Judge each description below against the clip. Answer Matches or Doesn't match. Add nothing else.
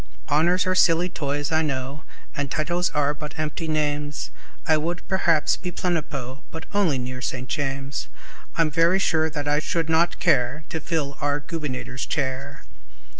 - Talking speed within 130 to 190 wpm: Matches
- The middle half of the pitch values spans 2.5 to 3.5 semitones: Matches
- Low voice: Doesn't match